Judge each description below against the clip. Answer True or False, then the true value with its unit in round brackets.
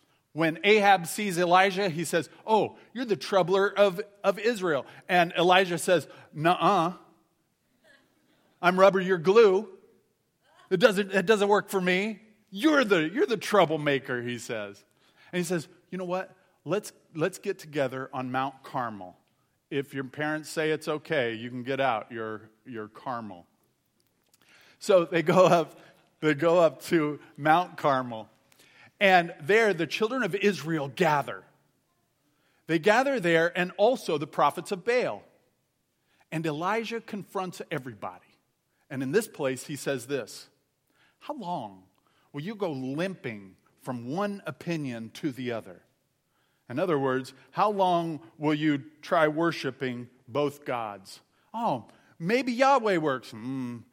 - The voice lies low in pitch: False (170 Hz)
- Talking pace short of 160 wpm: True (140 wpm)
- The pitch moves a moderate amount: False (6.2 semitones)